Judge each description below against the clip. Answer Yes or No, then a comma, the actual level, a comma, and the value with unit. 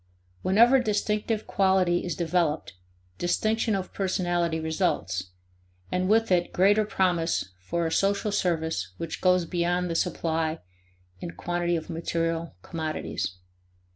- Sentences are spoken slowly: Yes, slow, 120 wpm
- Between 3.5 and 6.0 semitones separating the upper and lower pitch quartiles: No, average, 2.9 semitones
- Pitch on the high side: No, medium, 175 Hz